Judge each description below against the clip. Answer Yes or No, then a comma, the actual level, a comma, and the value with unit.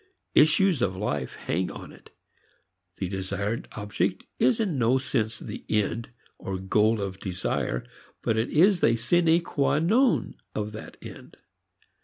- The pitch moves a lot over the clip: Yes, wide, 7.9 semitones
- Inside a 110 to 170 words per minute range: Yes, average, 145 wpm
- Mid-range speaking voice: No, low, 110 Hz